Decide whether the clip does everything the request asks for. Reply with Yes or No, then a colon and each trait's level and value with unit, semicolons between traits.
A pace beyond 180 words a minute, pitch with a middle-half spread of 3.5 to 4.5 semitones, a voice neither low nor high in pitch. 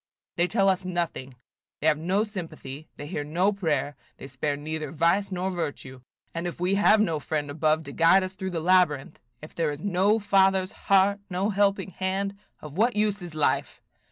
Yes: average, 190 wpm; average, 4.1 semitones; medium, 175 Hz